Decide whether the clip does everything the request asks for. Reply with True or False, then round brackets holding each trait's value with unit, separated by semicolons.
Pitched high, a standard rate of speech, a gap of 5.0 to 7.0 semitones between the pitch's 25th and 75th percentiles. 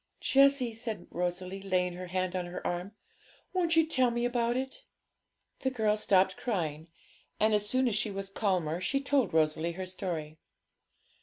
True (195 Hz; 165 wpm; 5.3 semitones)